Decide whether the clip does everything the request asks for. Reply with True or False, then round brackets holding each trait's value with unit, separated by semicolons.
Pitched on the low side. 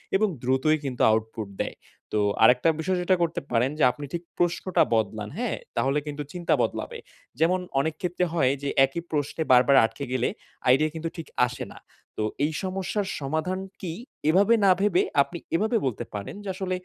False (155 Hz)